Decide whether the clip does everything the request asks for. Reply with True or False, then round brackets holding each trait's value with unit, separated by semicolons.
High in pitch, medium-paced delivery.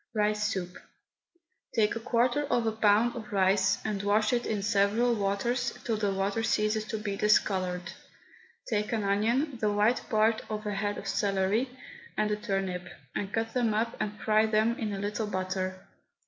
True (210 Hz; 175 wpm)